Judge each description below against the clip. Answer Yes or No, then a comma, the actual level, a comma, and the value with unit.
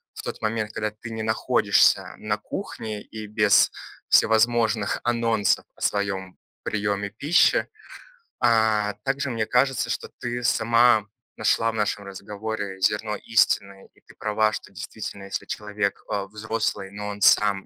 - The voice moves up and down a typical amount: No, narrow, 1.8 semitones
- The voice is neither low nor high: No, low, 110 Hz